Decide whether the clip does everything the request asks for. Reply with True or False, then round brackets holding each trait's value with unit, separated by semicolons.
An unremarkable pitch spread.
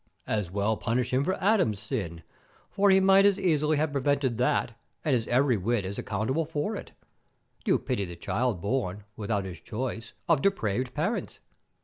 False (6.6 semitones)